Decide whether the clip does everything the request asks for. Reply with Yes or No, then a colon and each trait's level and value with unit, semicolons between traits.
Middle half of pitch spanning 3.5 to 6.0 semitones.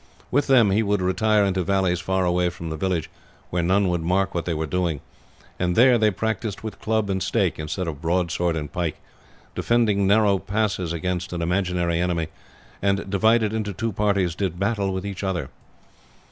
No: average, 2.8 semitones